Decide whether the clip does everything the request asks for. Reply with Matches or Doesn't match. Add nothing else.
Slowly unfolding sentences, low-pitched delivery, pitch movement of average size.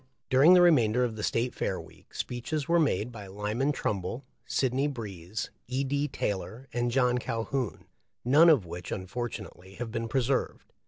Doesn't match